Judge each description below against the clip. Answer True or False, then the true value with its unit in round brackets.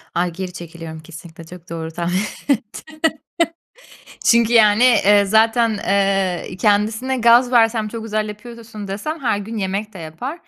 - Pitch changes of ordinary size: True (4.2 semitones)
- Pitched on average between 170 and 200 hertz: False (210 Hz)